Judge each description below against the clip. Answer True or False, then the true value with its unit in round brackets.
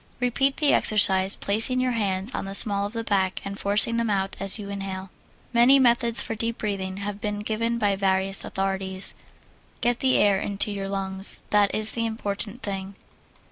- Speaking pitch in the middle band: False (205 Hz)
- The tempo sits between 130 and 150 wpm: False (180 wpm)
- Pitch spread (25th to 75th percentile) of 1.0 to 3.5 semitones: True (2.8 semitones)